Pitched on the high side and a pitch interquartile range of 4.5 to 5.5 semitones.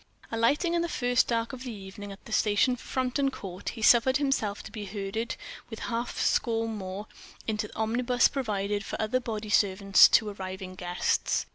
No: high, 220 Hz; average, 3.4 semitones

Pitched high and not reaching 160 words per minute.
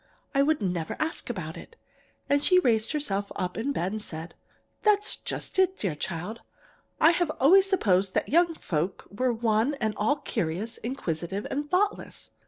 No: high, 230 Hz; average, 170 wpm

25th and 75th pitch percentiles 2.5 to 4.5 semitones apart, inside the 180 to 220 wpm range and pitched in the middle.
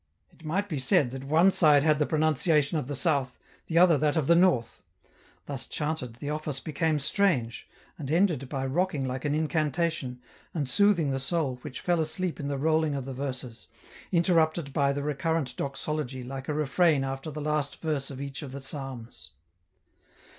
Yes: average, 3.1 semitones; average, 185 wpm; medium, 150 Hz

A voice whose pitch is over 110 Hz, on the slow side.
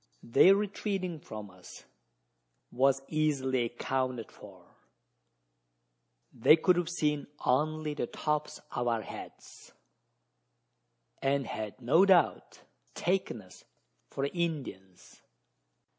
Yes: medium, 140 Hz; slow, 100 wpm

